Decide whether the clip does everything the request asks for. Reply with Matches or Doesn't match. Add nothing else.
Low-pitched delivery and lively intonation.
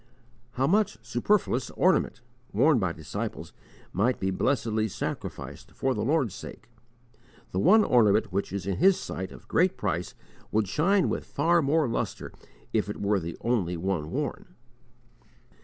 Matches